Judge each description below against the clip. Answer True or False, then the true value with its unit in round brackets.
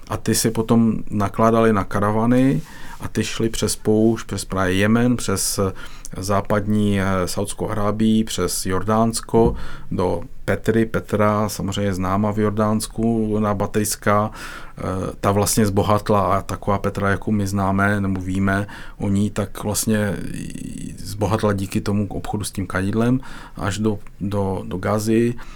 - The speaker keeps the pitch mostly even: True (2.0 semitones)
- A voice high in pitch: False (105 Hz)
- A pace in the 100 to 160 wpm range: True (145 wpm)